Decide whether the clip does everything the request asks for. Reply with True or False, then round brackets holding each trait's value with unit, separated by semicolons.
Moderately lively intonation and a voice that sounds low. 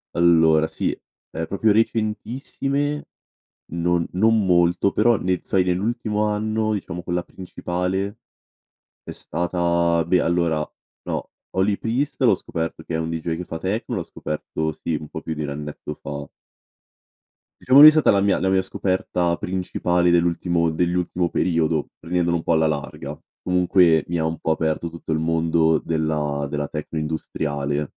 True (3.0 semitones; 85 Hz)